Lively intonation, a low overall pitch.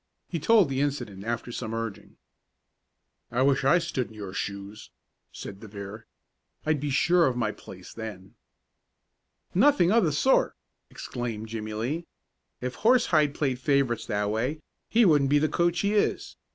Yes: wide, 6.3 semitones; low, 130 Hz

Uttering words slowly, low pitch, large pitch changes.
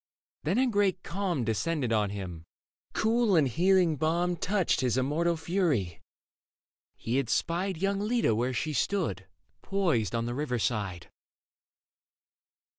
No: slow, 130 wpm; medium, 155 Hz; wide, 8.5 semitones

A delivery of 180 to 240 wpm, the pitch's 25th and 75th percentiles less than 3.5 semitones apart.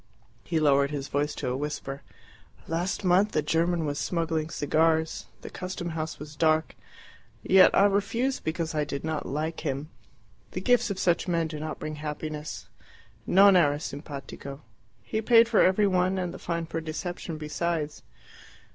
No: average, 165 wpm; average, 3.1 semitones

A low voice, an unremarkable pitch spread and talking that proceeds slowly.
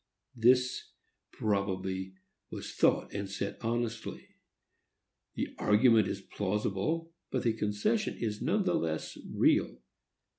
Yes: low, 105 Hz; average, 3.8 semitones; slow, 110 wpm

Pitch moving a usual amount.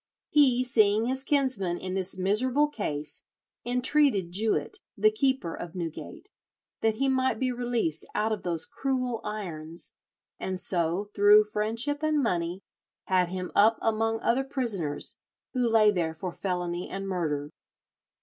No: wide, 5.8 semitones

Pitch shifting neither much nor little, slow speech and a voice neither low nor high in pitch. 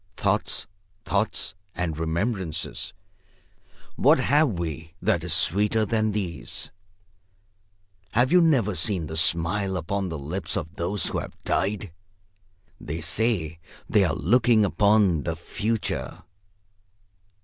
No: average, 4.6 semitones; slow, 115 wpm; very low, 95 Hz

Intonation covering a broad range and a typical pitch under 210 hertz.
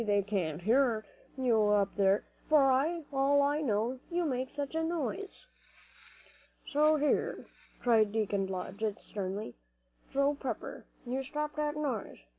No: wide, 6.1 semitones; very high, 255 Hz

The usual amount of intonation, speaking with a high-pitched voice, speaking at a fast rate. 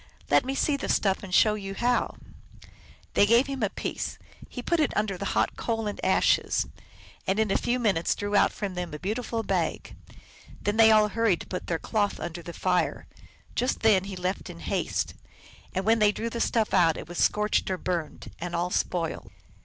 Yes: average, 3.7 semitones; high, 205 Hz; fast, 210 wpm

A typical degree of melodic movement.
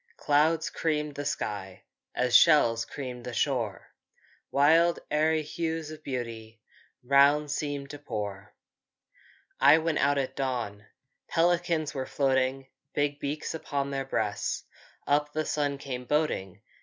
Yes: average, 3.3 semitones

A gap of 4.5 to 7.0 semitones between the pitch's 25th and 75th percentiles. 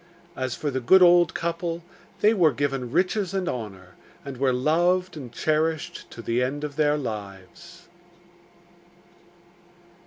Yes: wide, 5.4 semitones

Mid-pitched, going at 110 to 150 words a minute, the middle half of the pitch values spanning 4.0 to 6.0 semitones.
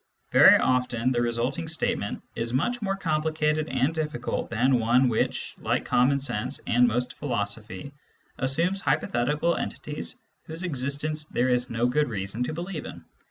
No: low, 130 Hz; average, 145 wpm; average, 4.3 semitones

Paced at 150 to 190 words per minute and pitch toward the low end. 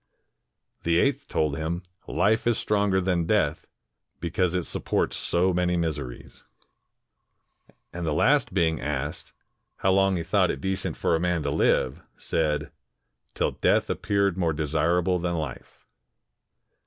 No: average, 140 wpm; very low, 85 Hz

